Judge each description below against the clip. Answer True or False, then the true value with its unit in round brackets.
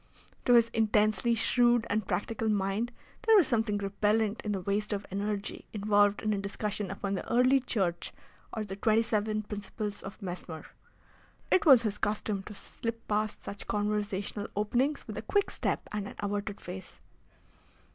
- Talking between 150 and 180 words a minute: True (165 wpm)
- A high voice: True (210 Hz)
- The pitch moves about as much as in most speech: False (1.9 semitones)